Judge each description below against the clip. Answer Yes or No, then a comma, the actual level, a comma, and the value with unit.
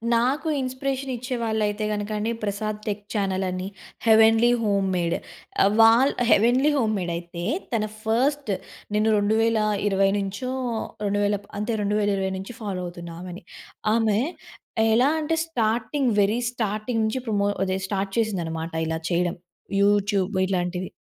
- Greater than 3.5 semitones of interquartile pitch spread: No, average, 2.8 semitones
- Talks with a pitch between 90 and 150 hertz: No, high, 210 Hz